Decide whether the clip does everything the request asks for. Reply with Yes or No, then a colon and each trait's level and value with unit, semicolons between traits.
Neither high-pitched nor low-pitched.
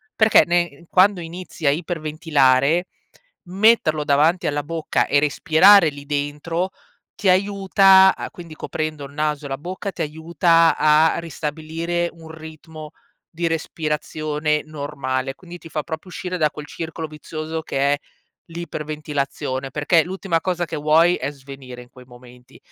Yes: medium, 155 Hz